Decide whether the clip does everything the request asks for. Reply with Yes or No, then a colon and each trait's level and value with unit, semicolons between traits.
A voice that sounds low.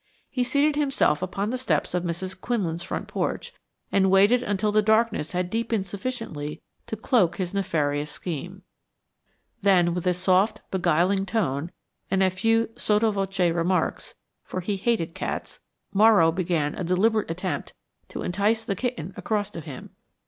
No: high, 190 Hz